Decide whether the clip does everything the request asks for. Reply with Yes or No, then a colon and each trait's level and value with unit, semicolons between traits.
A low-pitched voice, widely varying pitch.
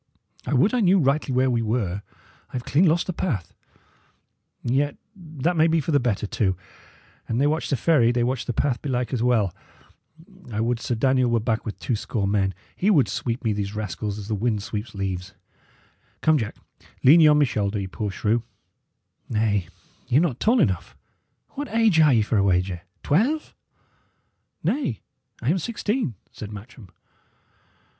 Yes: low, 120 Hz; wide, 6.5 semitones